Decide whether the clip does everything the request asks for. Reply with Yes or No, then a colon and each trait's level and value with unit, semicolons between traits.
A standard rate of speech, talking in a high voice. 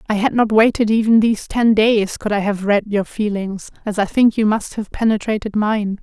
No: fast, 220 wpm; high, 210 Hz